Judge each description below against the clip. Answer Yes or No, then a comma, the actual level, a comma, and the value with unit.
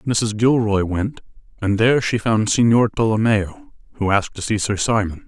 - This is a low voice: Yes, low, 110 Hz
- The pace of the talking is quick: No, average, 170 wpm